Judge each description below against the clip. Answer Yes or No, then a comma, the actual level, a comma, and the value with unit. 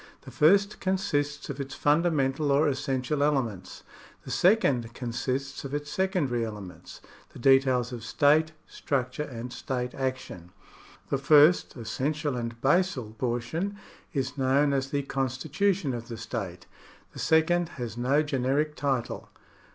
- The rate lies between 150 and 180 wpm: No, average, 140 wpm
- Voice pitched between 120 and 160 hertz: Yes, low, 135 Hz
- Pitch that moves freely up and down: No, average, 3.5 semitones